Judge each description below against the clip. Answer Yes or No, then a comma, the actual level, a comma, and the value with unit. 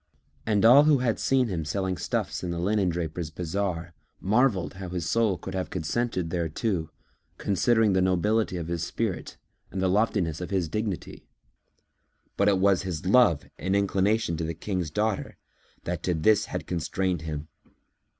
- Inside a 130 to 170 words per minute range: Yes, average, 160 wpm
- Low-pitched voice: Yes, very low, 95 Hz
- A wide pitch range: No, average, 3.6 semitones